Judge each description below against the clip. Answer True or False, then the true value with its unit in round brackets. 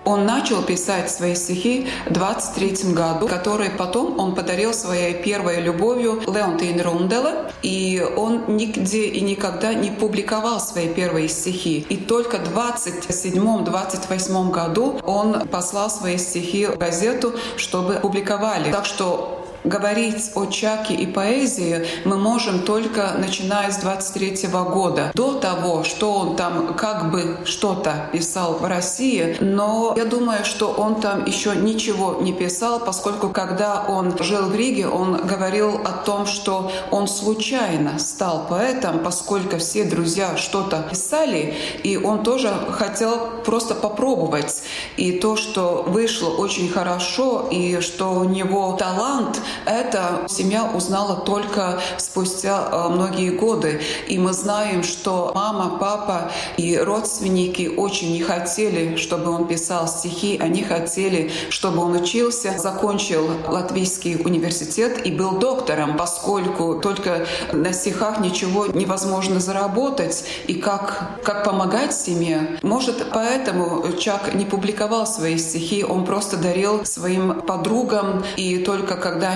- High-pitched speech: True (195 Hz)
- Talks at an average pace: True (130 wpm)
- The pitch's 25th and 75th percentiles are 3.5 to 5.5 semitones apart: False (3.1 semitones)